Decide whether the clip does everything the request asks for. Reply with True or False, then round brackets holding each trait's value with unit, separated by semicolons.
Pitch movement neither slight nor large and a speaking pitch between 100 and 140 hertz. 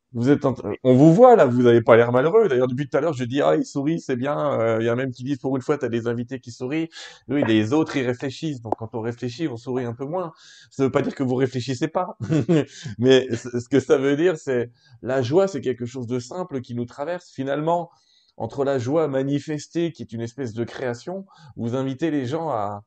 True (4.0 semitones; 135 Hz)